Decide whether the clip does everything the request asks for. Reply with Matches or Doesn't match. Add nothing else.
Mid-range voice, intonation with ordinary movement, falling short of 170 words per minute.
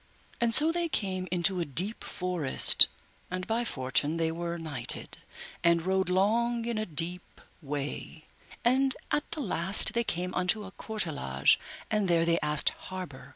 Matches